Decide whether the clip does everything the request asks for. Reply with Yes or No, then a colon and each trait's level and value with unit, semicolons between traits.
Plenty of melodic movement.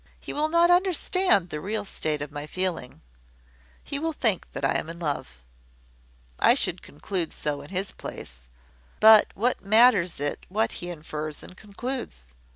Yes: wide, 7.9 semitones